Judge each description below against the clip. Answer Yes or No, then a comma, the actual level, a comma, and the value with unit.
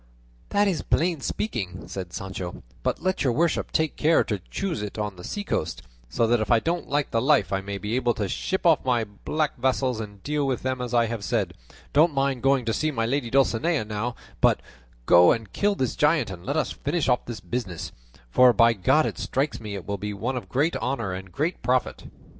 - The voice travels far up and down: Yes, wide, 5.7 semitones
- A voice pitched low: Yes, low, 120 Hz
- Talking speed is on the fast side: Yes, fast, 220 wpm